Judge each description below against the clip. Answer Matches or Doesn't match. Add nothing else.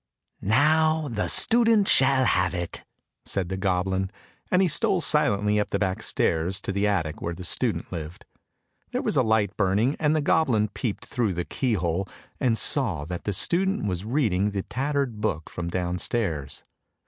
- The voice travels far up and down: Matches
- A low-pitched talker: Matches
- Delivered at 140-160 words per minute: Doesn't match